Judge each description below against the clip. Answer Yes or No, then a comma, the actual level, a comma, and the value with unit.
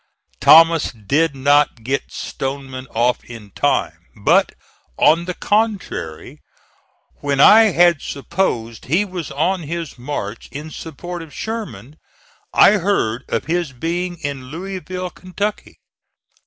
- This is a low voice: No, medium, 155 Hz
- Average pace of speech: No, slow, 120 wpm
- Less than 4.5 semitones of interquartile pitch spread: No, average, 5.2 semitones